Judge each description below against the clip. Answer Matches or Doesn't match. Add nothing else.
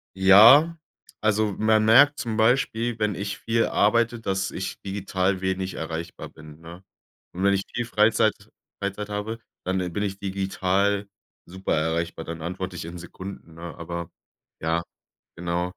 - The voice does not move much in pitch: Doesn't match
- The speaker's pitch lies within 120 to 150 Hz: Doesn't match